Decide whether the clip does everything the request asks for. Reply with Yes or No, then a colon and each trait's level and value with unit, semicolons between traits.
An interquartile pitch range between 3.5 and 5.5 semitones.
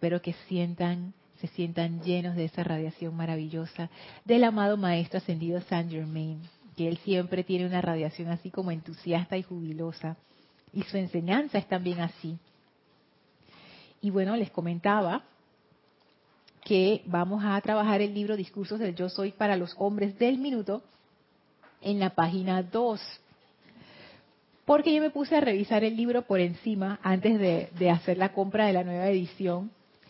No: average, 3.0 semitones